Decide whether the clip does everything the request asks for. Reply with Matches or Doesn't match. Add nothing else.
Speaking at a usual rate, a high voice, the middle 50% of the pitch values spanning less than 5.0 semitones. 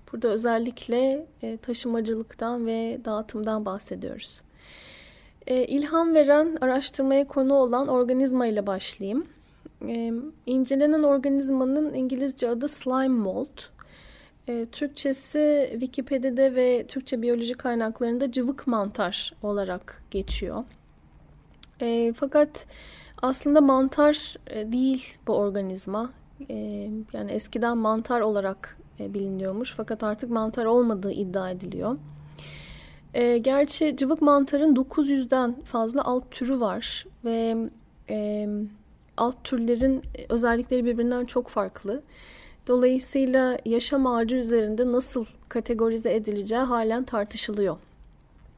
Doesn't match